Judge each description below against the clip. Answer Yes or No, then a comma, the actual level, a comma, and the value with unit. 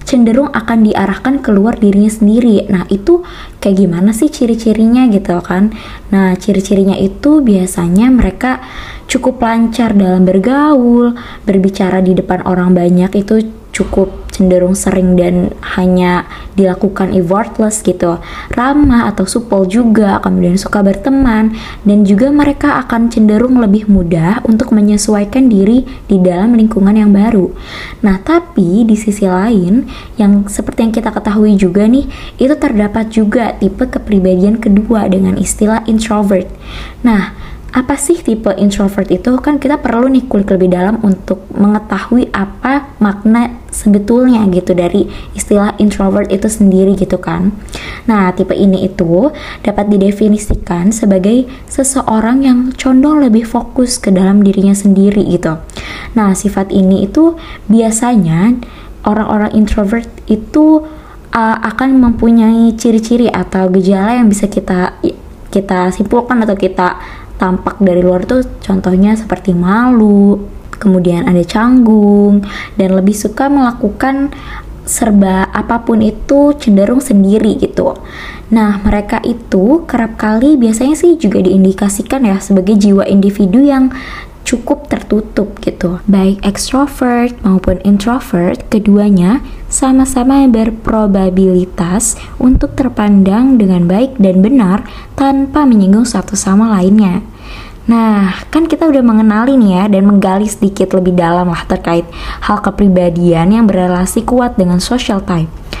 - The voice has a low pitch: No, high, 210 Hz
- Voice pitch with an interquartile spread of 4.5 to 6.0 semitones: No, average, 3.7 semitones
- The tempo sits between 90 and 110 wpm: No, average, 125 wpm